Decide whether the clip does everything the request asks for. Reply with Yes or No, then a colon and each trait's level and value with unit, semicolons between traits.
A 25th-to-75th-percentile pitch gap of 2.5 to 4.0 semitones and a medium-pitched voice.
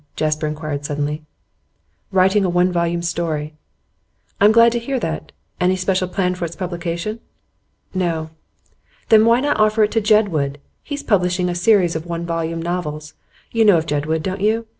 No: average, 4.4 semitones; medium, 180 Hz